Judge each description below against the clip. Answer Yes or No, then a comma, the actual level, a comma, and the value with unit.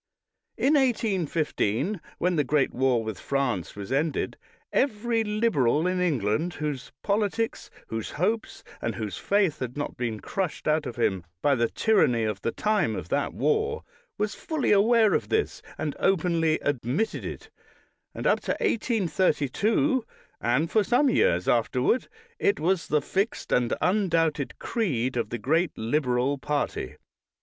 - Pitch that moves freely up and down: Yes, wide, 9.0 semitones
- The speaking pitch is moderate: Yes, medium, 160 Hz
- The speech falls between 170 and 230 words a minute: No, average, 145 wpm